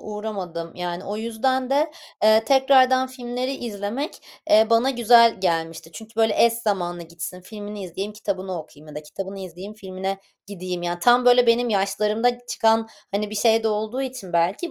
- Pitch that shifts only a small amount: No, average, 4.5 semitones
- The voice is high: Yes, high, 210 Hz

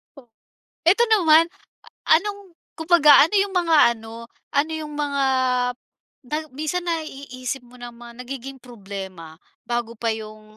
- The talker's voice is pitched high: Yes, very high, 270 Hz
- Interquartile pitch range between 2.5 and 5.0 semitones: No, wide, 5.4 semitones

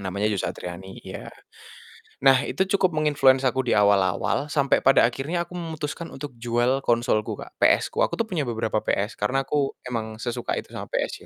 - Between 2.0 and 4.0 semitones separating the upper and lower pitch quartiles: No, average, 4.8 semitones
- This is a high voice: No, low, 130 Hz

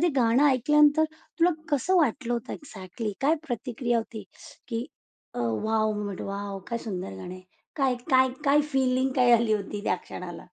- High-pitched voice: Yes, high, 235 Hz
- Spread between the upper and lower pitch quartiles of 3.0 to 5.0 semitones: Yes, average, 4.6 semitones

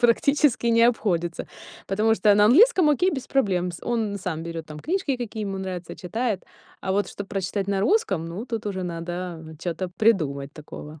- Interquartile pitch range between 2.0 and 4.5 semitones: No, average, 5.1 semitones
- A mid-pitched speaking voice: No, high, 200 Hz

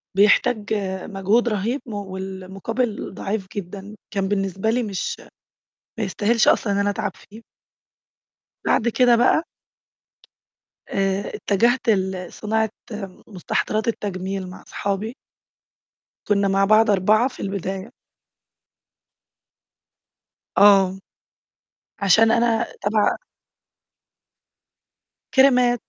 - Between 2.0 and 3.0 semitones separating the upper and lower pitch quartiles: Yes, narrow, 2.6 semitones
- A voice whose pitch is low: No, high, 205 Hz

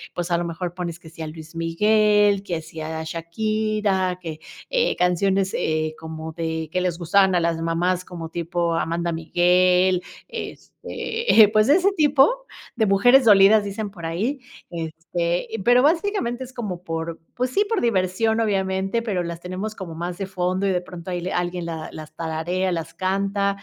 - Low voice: No, medium, 180 Hz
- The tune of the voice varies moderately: Yes, average, 3.9 semitones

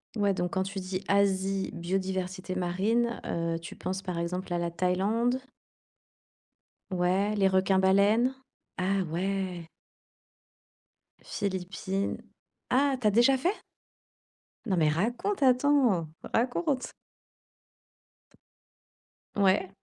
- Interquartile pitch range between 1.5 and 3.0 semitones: No, average, 3.6 semitones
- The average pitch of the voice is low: No, high, 195 Hz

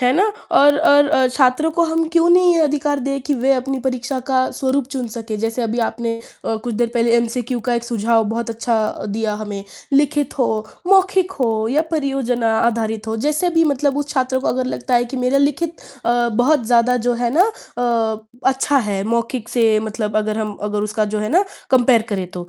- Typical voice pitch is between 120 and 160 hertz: No, very high, 250 Hz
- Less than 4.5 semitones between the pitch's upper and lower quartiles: Yes, average, 3.8 semitones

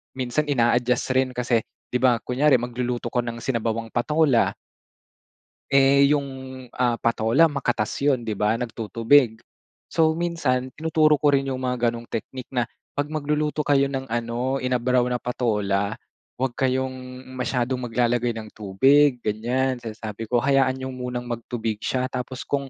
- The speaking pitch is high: No, low, 125 Hz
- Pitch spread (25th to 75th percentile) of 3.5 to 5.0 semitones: No, narrow, 2.4 semitones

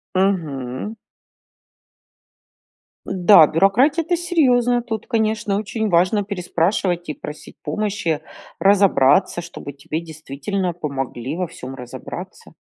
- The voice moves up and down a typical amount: No, wide, 5.7 semitones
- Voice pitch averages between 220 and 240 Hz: No, medium, 185 Hz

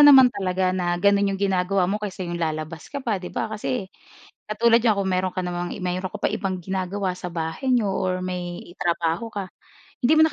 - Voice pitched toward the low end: No, medium, 185 Hz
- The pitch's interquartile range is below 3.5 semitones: Yes, average, 2.8 semitones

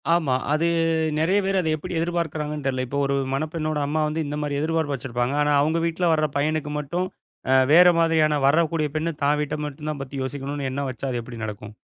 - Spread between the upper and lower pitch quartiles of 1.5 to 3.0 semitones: Yes, narrow, 2.5 semitones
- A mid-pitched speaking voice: Yes, medium, 150 Hz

